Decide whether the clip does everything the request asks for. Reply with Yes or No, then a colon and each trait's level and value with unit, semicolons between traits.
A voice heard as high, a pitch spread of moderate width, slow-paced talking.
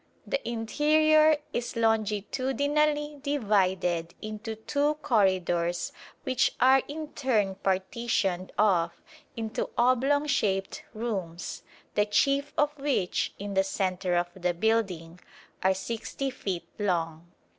No: high, 215 Hz; wide, 6.6 semitones; slow, 110 wpm